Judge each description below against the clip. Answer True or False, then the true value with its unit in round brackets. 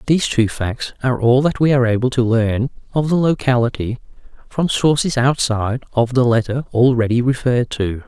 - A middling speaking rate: True (170 wpm)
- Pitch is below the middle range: True (125 Hz)